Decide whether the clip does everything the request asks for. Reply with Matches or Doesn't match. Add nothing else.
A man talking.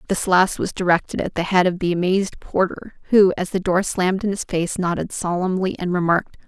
Doesn't match